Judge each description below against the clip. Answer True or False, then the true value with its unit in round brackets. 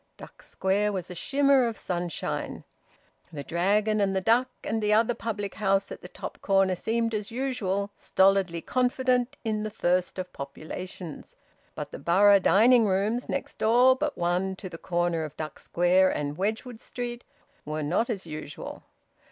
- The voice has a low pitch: False (200 Hz)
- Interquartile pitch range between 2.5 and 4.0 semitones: False (4.4 semitones)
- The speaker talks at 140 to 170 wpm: True (165 wpm)